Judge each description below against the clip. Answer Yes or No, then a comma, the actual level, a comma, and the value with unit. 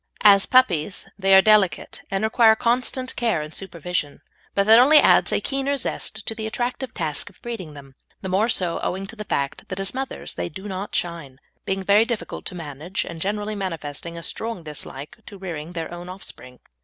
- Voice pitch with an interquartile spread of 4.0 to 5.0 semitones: Yes, average, 4.7 semitones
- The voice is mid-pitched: No, high, 195 Hz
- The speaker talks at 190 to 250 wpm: Yes, average, 195 wpm